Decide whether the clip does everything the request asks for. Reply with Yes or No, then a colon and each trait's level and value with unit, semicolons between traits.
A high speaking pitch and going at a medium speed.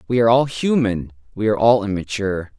No: low, 110 Hz; average, 185 wpm